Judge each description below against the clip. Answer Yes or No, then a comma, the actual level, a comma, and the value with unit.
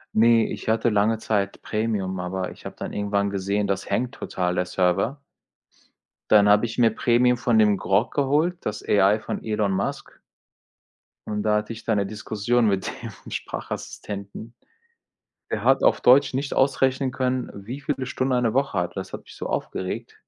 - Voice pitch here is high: No, low, 110 Hz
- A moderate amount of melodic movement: Yes, average, 3.8 semitones